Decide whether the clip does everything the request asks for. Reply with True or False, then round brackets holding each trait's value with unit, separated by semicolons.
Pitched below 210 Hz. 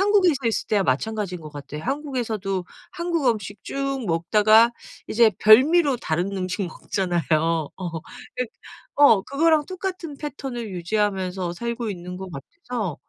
False (215 Hz)